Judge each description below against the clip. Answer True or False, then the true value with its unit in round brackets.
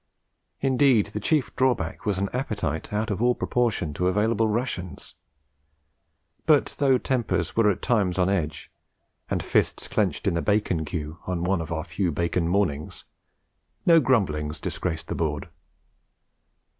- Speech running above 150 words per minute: False (145 wpm)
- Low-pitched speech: True (100 Hz)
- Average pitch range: False (6.2 semitones)